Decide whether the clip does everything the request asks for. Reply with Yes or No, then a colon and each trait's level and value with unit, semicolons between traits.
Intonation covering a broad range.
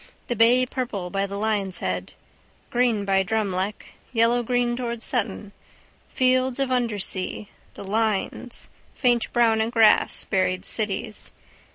No: average, 3.5 semitones